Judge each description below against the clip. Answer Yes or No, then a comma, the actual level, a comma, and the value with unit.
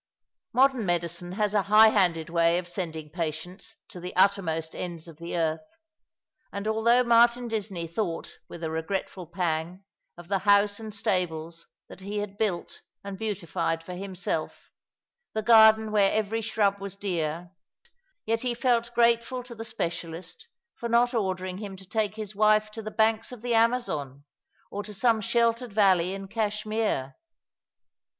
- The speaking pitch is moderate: No, high, 200 Hz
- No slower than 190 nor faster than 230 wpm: No, average, 160 wpm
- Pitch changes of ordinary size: Yes, average, 4.2 semitones